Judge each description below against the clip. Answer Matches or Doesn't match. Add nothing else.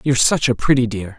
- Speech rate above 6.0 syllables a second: Matches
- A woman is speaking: Doesn't match